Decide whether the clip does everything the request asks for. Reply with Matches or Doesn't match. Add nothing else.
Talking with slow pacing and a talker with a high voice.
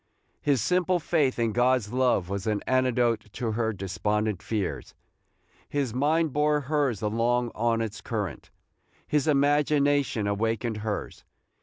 Doesn't match